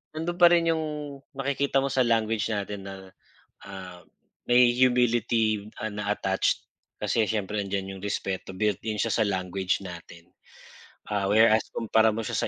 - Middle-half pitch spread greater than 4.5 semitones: No, average, 3.6 semitones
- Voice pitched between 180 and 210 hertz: No, low, 105 Hz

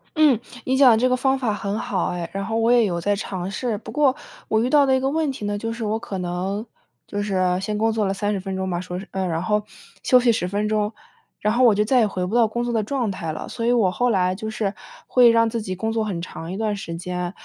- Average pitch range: Yes, average, 3.7 semitones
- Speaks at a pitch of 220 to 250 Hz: No, high, 210 Hz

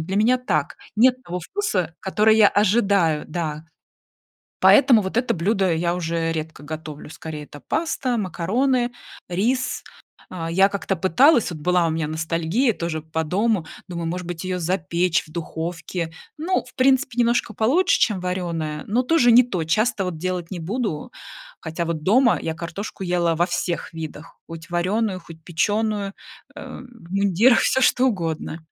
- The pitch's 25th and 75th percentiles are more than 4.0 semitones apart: Yes, wide, 5.5 semitones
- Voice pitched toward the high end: No, medium, 180 Hz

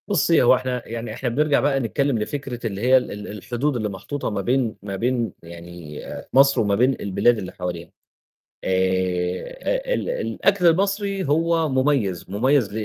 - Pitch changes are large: Yes, wide, 6.6 semitones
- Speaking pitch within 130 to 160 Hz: No, low, 120 Hz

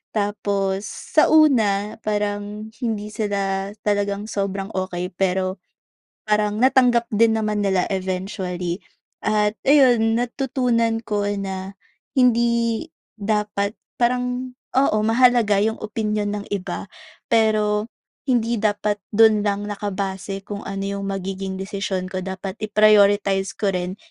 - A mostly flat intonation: Yes, narrow, 2.3 semitones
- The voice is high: Yes, high, 205 Hz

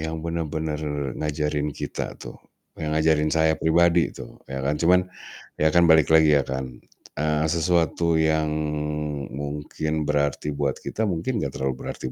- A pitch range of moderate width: No, narrow, 1.7 semitones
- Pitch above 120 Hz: No, very low, 80 Hz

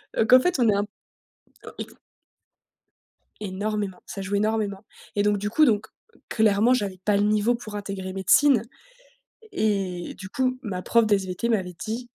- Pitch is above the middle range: Yes, high, 210 Hz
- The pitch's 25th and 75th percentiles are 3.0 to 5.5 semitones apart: No, narrow, 2.4 semitones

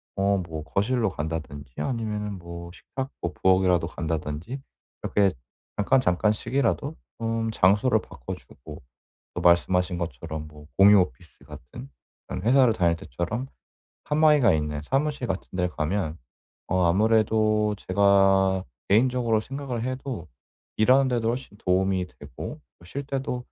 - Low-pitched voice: Yes, low, 100 Hz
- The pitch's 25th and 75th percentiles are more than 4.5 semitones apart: Yes, wide, 5.5 semitones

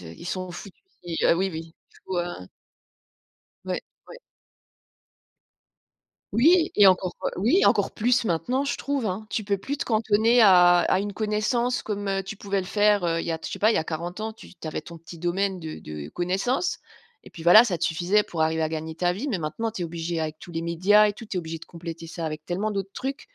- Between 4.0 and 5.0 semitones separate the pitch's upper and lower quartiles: Yes, average, 4.3 semitones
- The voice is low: No, medium, 185 Hz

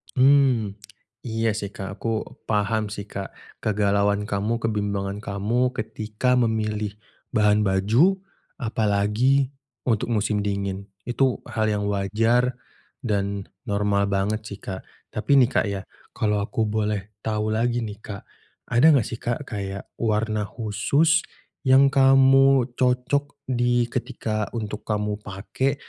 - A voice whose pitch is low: Yes, low, 110 Hz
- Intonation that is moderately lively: Yes, average, 3.1 semitones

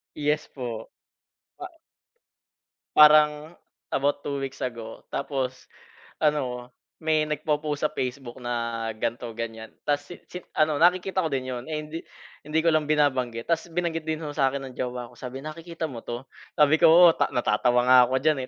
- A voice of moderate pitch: Yes, medium, 145 Hz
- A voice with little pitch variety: No, average, 3.8 semitones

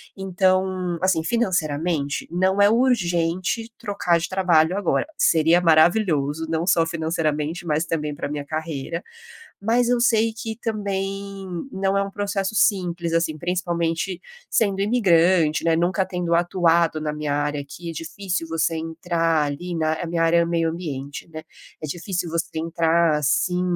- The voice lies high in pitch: No, medium, 170 Hz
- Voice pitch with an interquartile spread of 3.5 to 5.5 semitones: No, average, 3.0 semitones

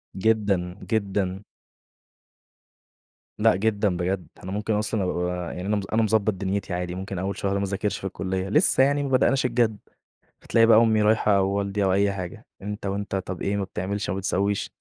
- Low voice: Yes, low, 100 Hz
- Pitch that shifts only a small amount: Yes, narrow, 2.2 semitones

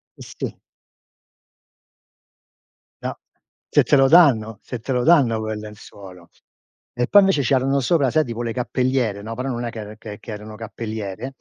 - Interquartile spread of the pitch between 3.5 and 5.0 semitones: Yes, average, 3.8 semitones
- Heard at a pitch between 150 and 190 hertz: No, low, 120 Hz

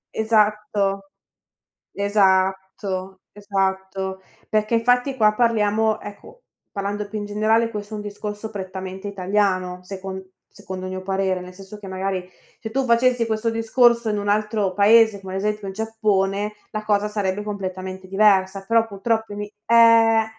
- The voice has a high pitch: Yes, high, 205 Hz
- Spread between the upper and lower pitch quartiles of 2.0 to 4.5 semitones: Yes, narrow, 2.4 semitones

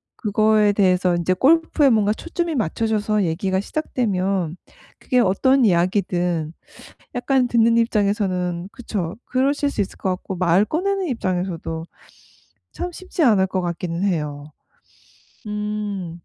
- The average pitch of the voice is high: Yes, high, 200 Hz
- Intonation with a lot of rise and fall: No, average, 5.0 semitones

